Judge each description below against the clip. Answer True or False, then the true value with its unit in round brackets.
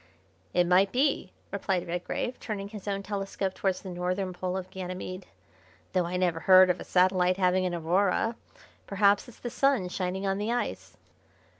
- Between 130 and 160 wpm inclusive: False (170 wpm)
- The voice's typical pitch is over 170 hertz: True (185 Hz)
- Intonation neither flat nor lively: False (1.7 semitones)